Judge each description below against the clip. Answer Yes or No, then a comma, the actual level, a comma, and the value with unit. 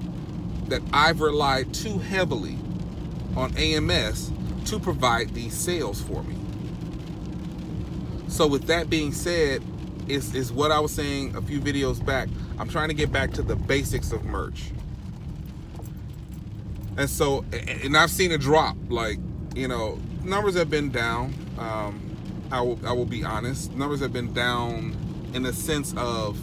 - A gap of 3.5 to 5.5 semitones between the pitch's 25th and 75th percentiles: Yes, average, 4.5 semitones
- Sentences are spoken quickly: No, average, 150 wpm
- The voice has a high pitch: No, low, 135 Hz